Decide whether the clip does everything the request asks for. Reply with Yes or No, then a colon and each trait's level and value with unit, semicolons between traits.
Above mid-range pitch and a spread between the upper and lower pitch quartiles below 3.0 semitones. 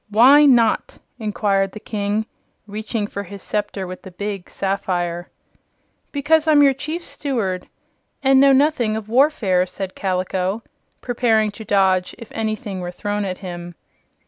No: high, 210 Hz; average, 4.4 semitones